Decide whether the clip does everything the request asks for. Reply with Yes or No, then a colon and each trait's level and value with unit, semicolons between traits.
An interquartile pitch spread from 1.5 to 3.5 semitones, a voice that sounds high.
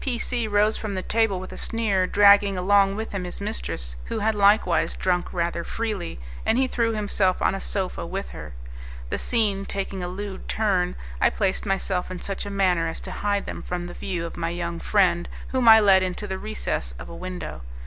Yes: narrow, 2.6 semitones; high, 195 Hz